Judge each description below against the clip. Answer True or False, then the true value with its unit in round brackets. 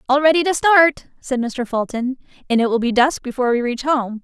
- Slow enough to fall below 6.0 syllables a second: True (5.5 syllables/s)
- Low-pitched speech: False (260 Hz)